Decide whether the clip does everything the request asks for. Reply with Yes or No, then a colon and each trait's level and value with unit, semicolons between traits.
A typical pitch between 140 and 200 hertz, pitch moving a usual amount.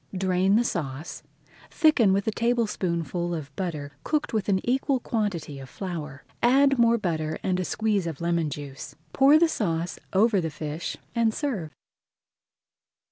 No: medium, 185 Hz; wide, 6.4 semitones